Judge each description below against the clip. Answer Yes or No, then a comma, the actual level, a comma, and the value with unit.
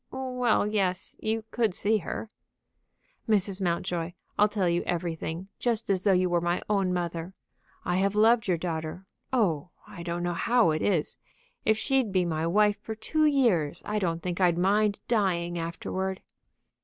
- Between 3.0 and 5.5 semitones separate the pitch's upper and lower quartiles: Yes, average, 3.7 semitones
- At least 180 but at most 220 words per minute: No, average, 165 wpm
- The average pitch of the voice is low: No, high, 190 Hz